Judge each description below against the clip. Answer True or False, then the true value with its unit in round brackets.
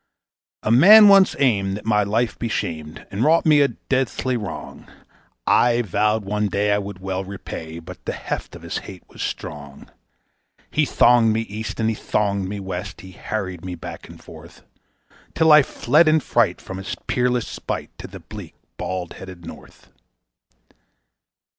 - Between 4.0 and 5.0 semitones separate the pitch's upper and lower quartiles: True (4.4 semitones)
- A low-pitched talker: True (105 Hz)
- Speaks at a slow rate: False (170 wpm)